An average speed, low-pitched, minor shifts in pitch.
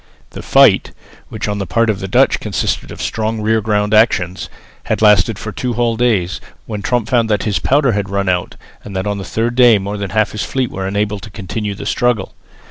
No: fast, 220 wpm; low, 105 Hz; narrow, 2.3 semitones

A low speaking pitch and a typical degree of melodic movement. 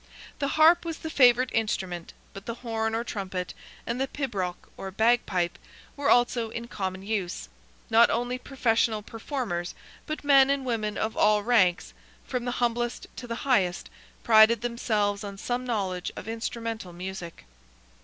No: high, 225 Hz; average, 3.8 semitones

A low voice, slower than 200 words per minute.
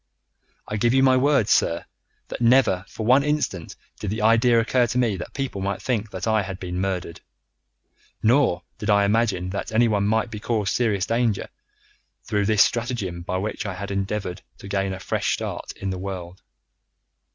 Yes: low, 105 Hz; average, 180 wpm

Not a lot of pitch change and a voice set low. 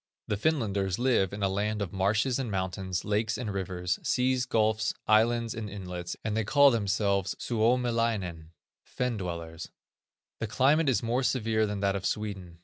No: average, 3.4 semitones; low, 105 Hz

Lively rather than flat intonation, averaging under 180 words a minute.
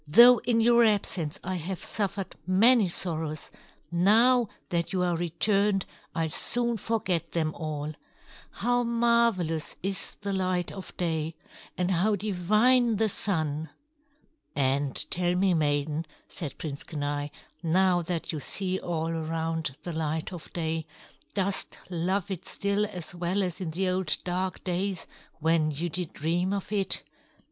No: average, 3.7 semitones; average, 145 wpm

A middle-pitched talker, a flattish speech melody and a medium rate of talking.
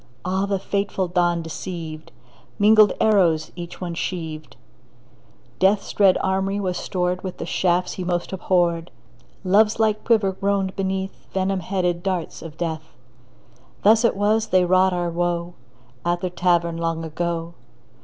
Yes: medium, 180 Hz; narrow, 2.2 semitones; average, 145 wpm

